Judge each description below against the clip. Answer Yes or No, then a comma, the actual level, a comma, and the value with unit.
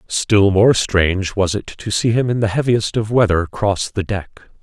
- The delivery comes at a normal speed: No, fast, 210 wpm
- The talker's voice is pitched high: No, low, 105 Hz